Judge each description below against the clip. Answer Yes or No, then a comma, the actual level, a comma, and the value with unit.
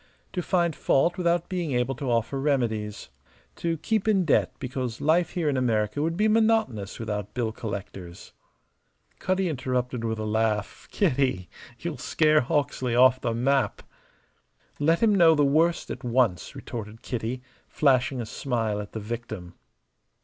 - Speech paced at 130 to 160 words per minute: Yes, average, 150 wpm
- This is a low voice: Yes, low, 130 Hz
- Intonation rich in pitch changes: Yes, wide, 6.2 semitones